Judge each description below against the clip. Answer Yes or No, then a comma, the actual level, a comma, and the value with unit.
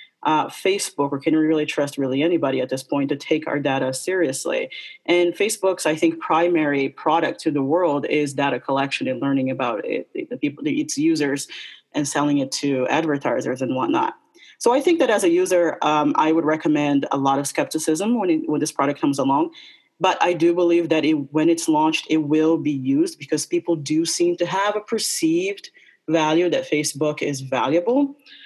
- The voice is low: No, medium, 160 Hz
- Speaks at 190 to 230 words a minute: Yes, average, 195 wpm